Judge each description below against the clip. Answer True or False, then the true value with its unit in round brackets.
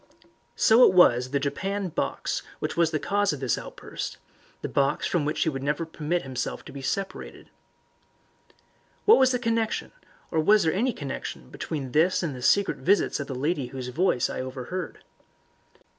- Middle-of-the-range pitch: True (160 Hz)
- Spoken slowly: False (180 wpm)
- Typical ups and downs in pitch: False (6.3 semitones)